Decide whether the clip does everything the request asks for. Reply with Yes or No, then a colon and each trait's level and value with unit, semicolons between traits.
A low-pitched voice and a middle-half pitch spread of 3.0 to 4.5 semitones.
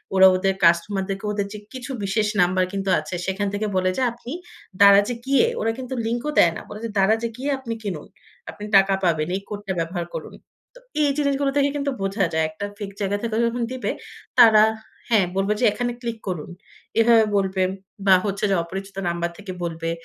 No: high, 200 Hz; average, 3.7 semitones